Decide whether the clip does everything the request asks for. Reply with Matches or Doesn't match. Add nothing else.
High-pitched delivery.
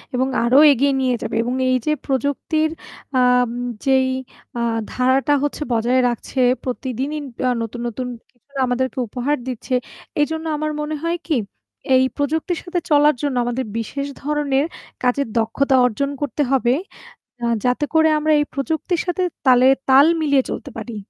Matches